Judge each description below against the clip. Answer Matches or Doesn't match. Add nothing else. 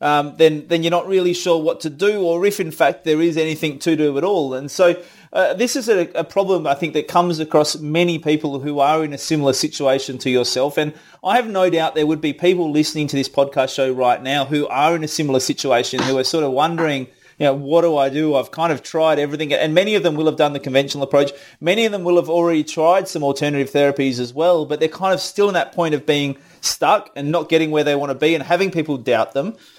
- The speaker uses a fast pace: Matches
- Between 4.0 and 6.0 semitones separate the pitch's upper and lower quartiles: Doesn't match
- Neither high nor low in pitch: Matches